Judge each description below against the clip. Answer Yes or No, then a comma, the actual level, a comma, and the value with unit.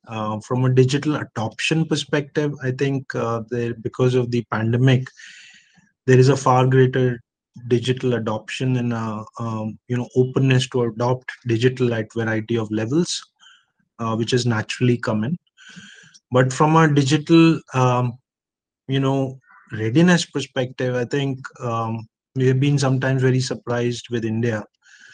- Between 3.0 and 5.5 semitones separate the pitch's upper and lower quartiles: No, narrow, 2.6 semitones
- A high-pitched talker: No, low, 125 Hz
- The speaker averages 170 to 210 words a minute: No, average, 140 wpm